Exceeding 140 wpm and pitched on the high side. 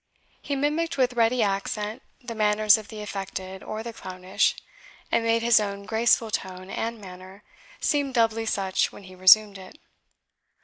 Yes: average, 160 wpm; high, 215 Hz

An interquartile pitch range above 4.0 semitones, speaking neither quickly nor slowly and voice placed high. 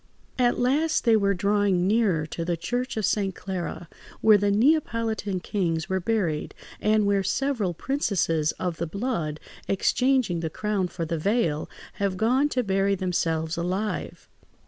Yes: average, 4.6 semitones; average, 150 wpm; high, 200 Hz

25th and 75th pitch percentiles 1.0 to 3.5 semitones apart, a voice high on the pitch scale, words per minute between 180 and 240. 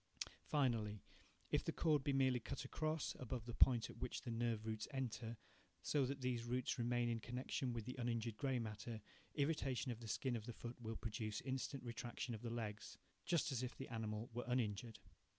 No: narrow, 2.6 semitones; low, 120 Hz; average, 195 wpm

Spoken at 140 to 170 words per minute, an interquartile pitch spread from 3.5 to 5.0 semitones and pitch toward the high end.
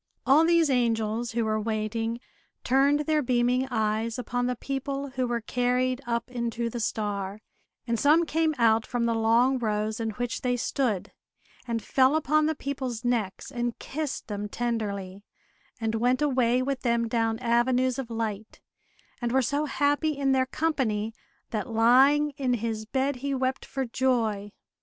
No: average, 160 wpm; average, 2.9 semitones; high, 245 Hz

